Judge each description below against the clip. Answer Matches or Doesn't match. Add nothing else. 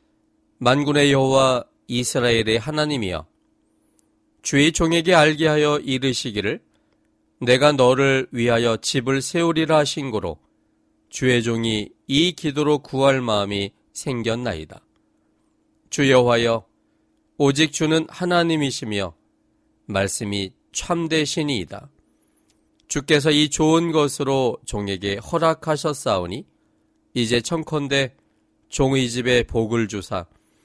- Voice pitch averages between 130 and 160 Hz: Matches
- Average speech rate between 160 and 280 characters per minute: Matches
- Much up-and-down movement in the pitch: Doesn't match